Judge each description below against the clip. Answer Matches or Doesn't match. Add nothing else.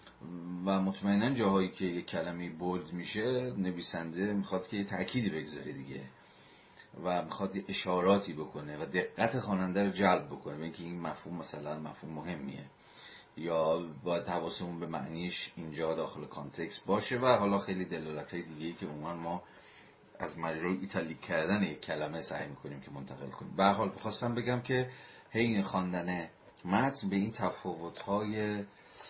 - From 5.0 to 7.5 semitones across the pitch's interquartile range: Doesn't match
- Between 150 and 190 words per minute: Matches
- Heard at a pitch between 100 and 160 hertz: Doesn't match